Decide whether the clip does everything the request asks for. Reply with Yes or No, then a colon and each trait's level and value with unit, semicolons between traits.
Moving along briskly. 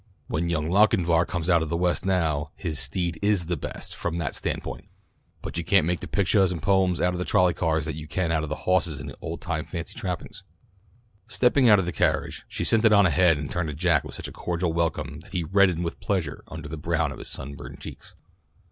Yes: fast, 230 wpm